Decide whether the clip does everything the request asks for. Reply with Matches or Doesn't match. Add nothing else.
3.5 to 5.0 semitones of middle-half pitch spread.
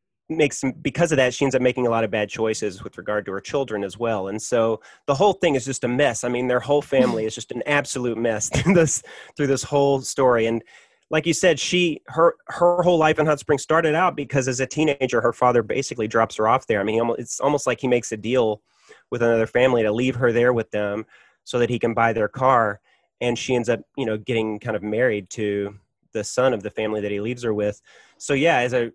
Matches